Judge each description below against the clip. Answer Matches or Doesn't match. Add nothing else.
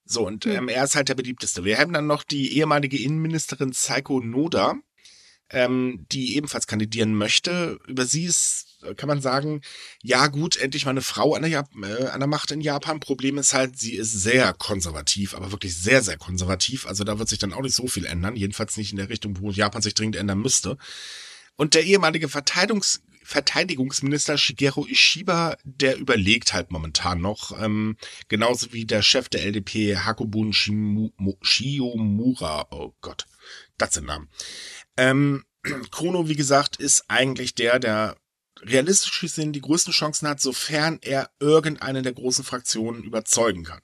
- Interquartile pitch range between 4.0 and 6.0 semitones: Matches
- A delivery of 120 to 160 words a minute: Doesn't match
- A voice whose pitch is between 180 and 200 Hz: Doesn't match